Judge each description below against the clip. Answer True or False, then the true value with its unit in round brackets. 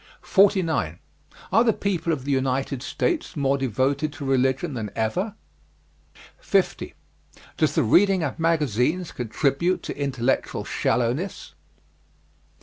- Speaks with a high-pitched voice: False (140 Hz)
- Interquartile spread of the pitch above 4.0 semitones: True (5.2 semitones)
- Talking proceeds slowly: True (115 wpm)